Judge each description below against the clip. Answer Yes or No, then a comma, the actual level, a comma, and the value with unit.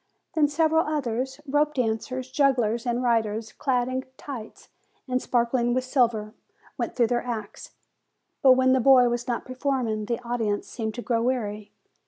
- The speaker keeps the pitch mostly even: Yes, narrow, 2.3 semitones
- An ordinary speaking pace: Yes, average, 160 wpm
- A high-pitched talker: Yes, high, 245 Hz